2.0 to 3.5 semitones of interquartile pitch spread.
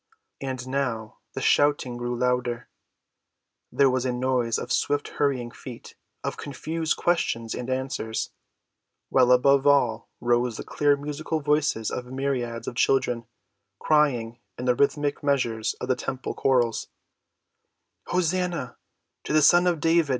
Yes: average, 3.1 semitones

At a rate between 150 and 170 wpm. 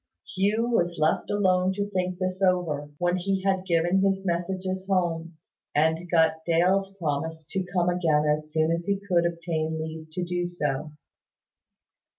Yes: average, 160 wpm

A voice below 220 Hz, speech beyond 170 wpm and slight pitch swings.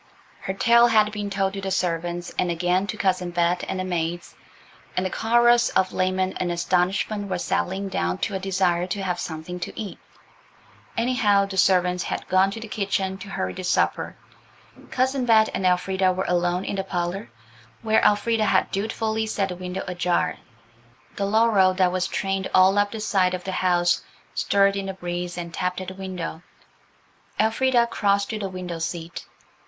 Yes: high, 190 Hz; average, 180 wpm; narrow, 2.3 semitones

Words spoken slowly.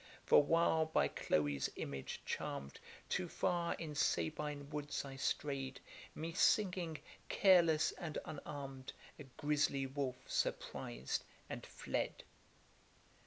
Yes: slow, 110 wpm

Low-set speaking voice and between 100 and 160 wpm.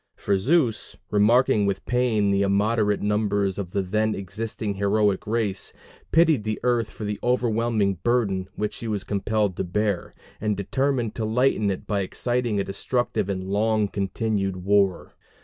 Yes: low, 105 Hz; average, 155 wpm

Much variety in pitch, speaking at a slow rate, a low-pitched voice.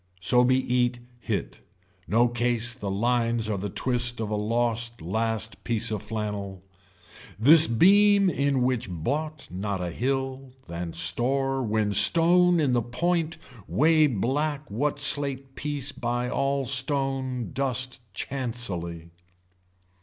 No: average, 4.1 semitones; slow, 130 wpm; low, 120 Hz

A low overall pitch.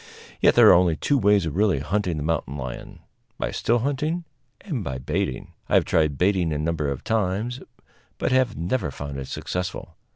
Yes: very low, 90 Hz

